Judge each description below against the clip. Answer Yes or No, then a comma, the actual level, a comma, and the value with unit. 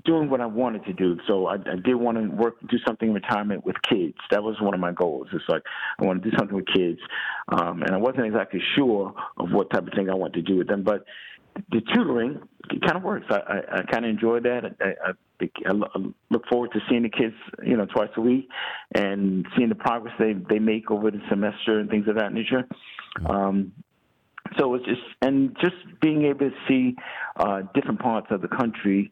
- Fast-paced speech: Yes, fast, 225 wpm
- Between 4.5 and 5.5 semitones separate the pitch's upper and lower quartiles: No, average, 3.7 semitones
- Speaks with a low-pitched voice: Yes, low, 110 Hz